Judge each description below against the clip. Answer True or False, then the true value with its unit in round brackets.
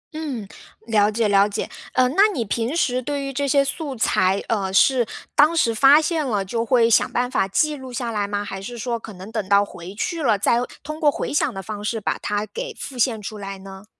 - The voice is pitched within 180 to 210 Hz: False (230 Hz)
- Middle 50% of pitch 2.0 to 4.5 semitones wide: False (5.1 semitones)